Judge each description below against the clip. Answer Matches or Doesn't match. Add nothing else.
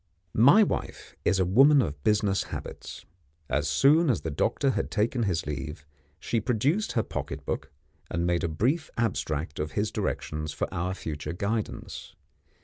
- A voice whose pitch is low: Matches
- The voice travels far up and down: Matches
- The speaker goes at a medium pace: Matches